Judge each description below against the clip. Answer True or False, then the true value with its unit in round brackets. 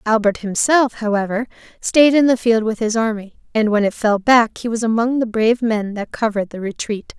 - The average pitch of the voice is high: True (225 Hz)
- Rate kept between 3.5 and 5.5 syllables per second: True (5.3 syllables/s)